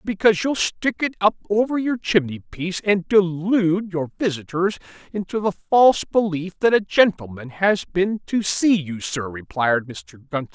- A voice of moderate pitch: Yes, medium, 180 Hz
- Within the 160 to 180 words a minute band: Yes, average, 165 wpm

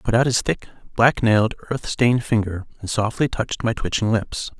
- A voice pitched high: No, low, 115 Hz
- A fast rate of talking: Yes, fast, 210 wpm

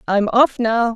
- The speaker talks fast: No, average, 190 wpm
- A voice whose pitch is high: Yes, high, 230 Hz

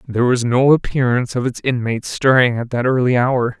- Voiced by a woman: No, male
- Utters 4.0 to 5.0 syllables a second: No, 5.7 syllables/s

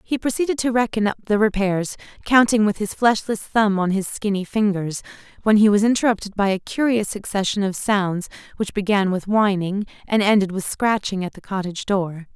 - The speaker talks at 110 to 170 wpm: No, average, 185 wpm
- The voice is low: No, high, 205 Hz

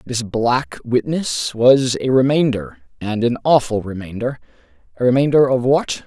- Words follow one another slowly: Yes, slow, 130 wpm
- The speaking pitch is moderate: No, low, 120 Hz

